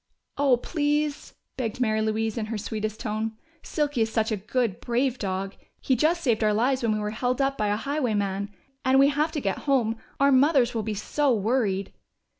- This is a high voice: Yes, high, 230 Hz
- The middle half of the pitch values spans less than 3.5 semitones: No, average, 4.2 semitones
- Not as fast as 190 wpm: No, average, 200 wpm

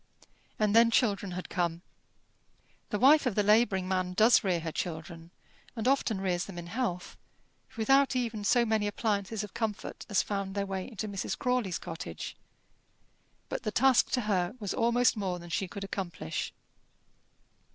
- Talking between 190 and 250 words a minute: No, average, 160 wpm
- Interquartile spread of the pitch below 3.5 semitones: No, average, 3.8 semitones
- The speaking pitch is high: Yes, high, 205 Hz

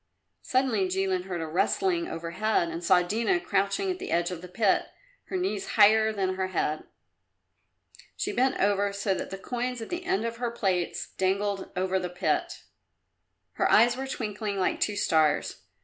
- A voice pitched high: Yes, high, 200 Hz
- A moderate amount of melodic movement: Yes, average, 4.3 semitones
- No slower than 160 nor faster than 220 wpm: Yes, average, 175 wpm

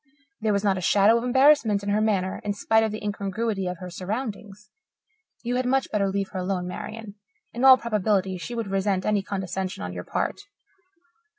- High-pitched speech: Yes, high, 205 Hz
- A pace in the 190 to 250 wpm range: Yes, average, 195 wpm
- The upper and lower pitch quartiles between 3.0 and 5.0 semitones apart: No, narrow, 2.6 semitones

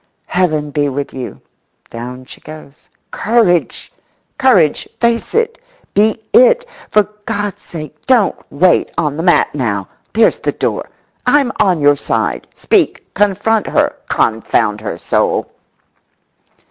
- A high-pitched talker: No, medium, 175 Hz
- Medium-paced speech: No, slow, 125 wpm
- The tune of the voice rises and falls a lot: Yes, wide, 7.5 semitones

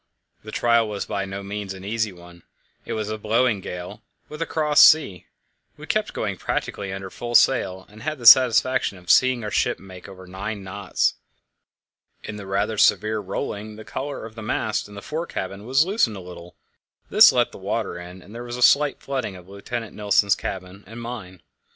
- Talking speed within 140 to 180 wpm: No, average, 200 wpm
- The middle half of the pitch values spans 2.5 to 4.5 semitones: Yes, average, 3.8 semitones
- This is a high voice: No, low, 105 Hz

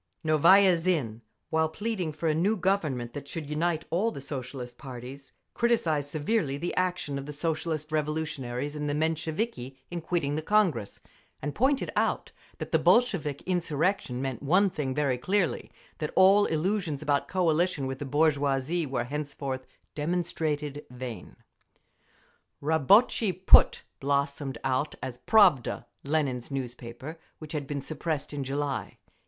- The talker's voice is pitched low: No, medium, 150 Hz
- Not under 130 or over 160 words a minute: Yes, average, 140 wpm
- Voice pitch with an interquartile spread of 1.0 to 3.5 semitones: No, average, 4.0 semitones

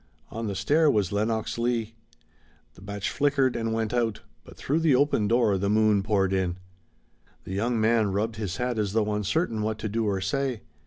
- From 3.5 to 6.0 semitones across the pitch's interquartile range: No, average, 2.8 semitones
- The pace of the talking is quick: No, average, 195 wpm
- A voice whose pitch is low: Yes, low, 110 Hz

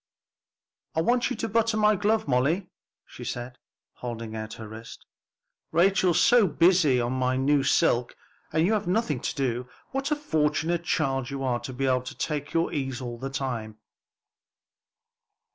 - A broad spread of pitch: Yes, wide, 6.4 semitones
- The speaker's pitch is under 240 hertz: Yes, medium, 140 Hz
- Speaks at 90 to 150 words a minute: No, average, 165 wpm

